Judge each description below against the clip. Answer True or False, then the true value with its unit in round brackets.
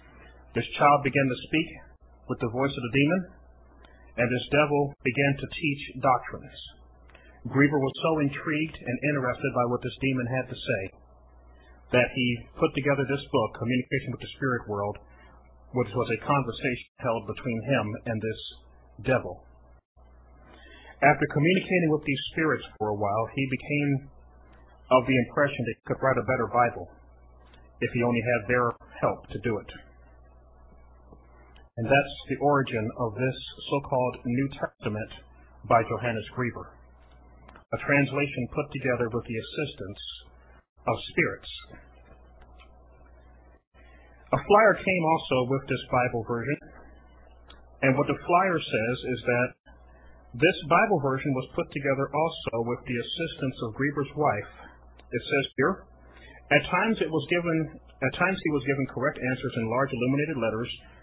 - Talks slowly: False (145 wpm)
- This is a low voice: True (120 Hz)